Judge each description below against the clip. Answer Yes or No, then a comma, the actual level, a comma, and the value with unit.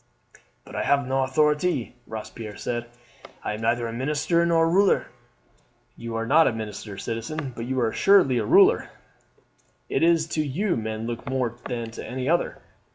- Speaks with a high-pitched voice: No, low, 130 Hz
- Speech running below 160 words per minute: No, average, 175 wpm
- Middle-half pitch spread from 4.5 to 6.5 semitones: Yes, wide, 5.5 semitones